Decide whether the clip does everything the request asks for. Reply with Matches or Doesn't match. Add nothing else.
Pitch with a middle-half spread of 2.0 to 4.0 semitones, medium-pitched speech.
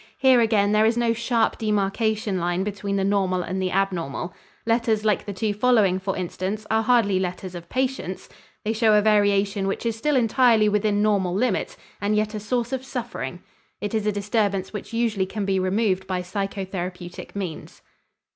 Doesn't match